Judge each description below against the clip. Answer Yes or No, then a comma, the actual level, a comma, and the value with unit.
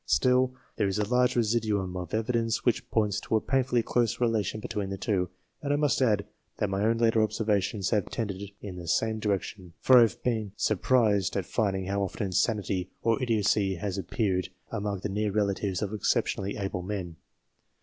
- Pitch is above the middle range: No, low, 105 Hz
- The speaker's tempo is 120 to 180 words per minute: No, average, 190 wpm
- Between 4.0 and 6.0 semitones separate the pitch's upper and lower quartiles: No, average, 2.8 semitones